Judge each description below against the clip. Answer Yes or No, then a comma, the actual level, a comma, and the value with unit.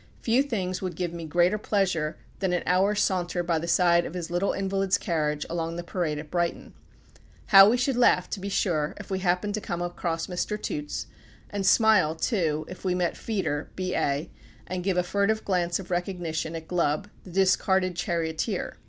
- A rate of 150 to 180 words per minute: No, average, 190 wpm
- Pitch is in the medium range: Yes, medium, 180 Hz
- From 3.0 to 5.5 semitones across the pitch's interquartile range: No, narrow, 2.6 semitones